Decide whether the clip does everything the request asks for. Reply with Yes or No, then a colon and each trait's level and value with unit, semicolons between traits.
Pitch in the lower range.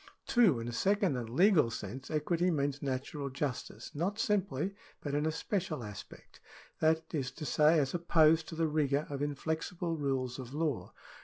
No: medium, 150 Hz